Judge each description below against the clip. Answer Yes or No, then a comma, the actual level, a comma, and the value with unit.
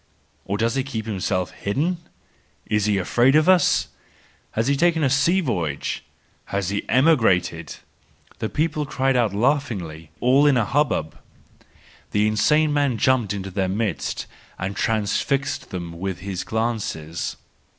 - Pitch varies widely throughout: Yes, wide, 6.4 semitones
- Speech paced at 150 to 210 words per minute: No, average, 140 wpm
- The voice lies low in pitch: Yes, low, 110 Hz